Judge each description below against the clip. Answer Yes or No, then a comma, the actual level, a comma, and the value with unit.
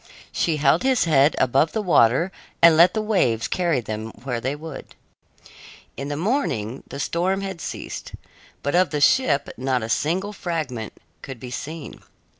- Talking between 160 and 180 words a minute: Yes, average, 165 wpm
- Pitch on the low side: No, medium, 150 Hz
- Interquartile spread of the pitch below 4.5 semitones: No, wide, 5.6 semitones